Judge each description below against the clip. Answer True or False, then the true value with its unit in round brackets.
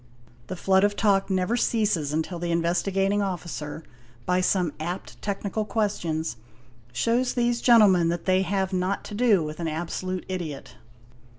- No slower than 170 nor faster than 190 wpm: False (160 wpm)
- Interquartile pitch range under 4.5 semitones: True (3.3 semitones)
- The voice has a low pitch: False (185 Hz)